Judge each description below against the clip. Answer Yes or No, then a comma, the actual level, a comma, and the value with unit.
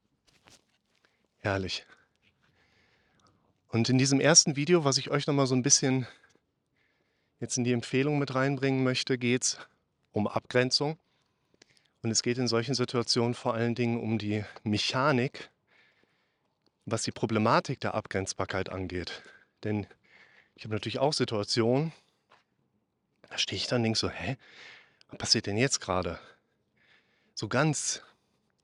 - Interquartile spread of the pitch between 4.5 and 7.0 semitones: No, average, 3.7 semitones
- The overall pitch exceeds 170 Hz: No, low, 120 Hz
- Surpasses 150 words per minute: No, average, 130 wpm